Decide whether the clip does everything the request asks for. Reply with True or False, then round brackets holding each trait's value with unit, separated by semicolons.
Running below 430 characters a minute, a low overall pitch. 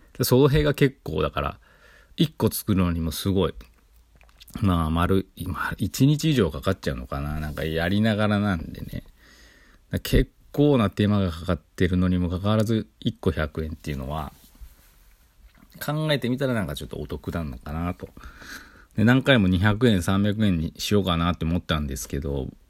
True (310 characters per minute; 90 Hz)